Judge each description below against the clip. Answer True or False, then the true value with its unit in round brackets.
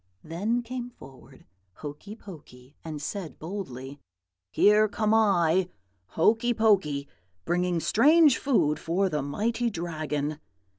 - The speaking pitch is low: False (180 Hz)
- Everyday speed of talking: False (110 wpm)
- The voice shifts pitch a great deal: True (6.6 semitones)